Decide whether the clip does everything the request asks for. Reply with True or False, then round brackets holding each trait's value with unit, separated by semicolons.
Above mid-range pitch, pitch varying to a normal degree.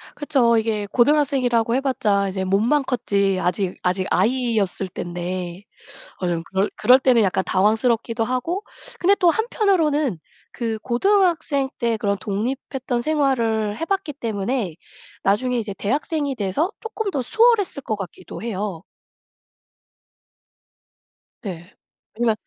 False (235 Hz; 6.0 semitones)